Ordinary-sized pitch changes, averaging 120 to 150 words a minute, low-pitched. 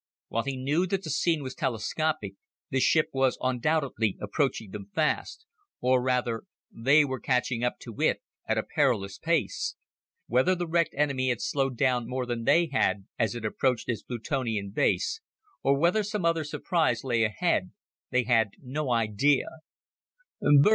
No: average, 4.9 semitones; average, 160 wpm; low, 130 Hz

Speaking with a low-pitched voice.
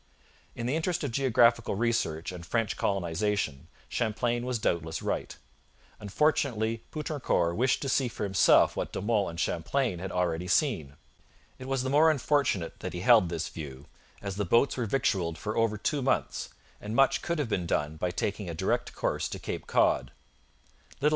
Yes: low, 110 Hz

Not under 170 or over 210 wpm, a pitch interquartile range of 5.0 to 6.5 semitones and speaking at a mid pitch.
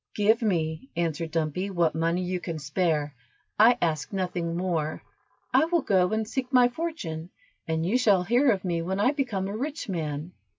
Yes: average, 180 wpm; wide, 5.4 semitones; medium, 180 Hz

